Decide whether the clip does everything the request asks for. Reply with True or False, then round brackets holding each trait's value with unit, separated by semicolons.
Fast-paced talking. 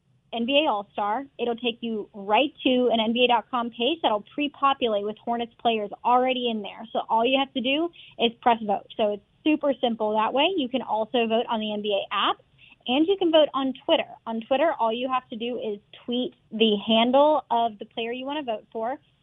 True (210 wpm)